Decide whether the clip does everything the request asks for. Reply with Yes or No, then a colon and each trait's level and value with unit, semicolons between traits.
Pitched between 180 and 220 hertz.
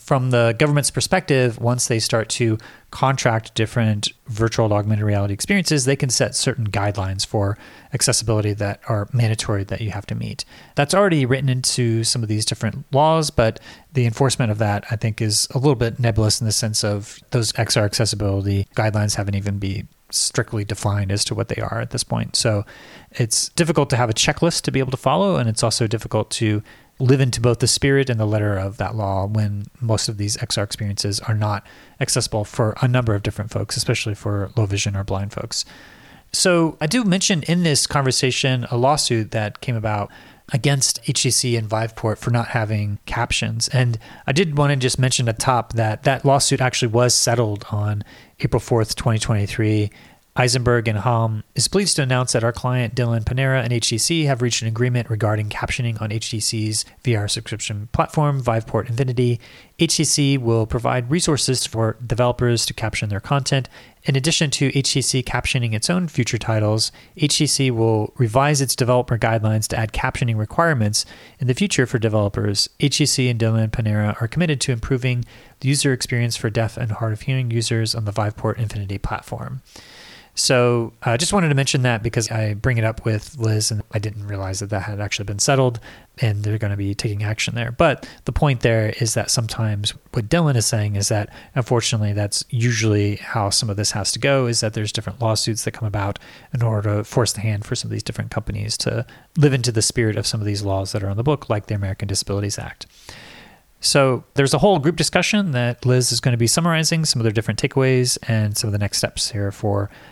No: low, 115 Hz